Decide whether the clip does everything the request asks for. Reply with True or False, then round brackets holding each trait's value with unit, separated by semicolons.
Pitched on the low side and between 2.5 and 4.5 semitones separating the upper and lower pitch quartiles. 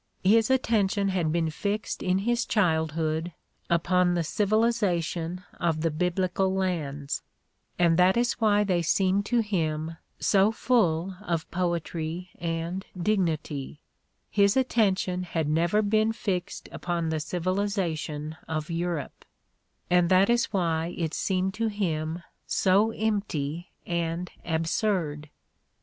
False (180 Hz; 3.7 semitones)